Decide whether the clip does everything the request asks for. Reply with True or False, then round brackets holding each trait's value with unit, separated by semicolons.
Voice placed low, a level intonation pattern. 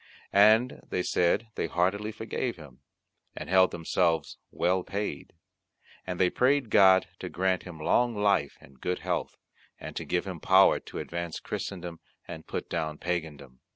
False (90 Hz; 3.5 semitones)